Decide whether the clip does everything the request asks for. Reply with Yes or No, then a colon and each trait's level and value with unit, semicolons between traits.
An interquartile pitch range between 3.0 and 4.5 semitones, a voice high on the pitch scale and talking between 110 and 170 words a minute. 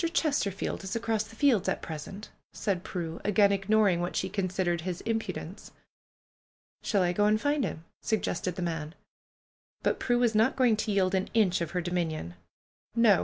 No: average, 3.8 semitones; high, 195 Hz; average, 180 wpm